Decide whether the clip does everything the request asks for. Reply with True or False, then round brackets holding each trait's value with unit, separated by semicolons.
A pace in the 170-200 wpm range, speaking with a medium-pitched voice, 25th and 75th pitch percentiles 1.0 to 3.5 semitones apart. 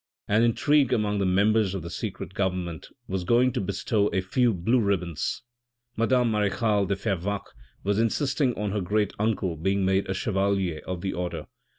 False (175 wpm; 100 Hz; 2.9 semitones)